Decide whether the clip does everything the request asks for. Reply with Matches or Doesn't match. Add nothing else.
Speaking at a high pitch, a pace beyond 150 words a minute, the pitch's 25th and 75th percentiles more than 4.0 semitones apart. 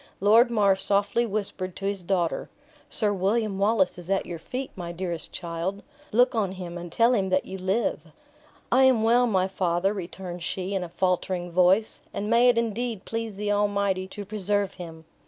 Doesn't match